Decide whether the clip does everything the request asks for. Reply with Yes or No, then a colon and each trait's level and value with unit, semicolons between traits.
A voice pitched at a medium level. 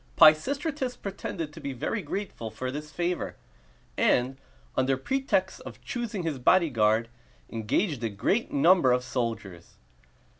Yes: medium, 150 Hz